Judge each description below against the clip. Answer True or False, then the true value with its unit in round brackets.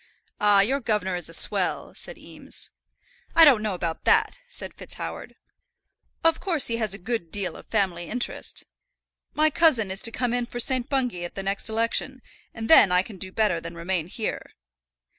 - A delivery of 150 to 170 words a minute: False (185 wpm)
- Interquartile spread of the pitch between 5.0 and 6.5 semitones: True (5.3 semitones)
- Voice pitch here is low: False (220 Hz)